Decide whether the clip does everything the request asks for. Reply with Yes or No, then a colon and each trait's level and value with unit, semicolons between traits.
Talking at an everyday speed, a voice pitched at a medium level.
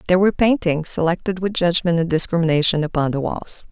Yes: average, 180 wpm; medium, 170 Hz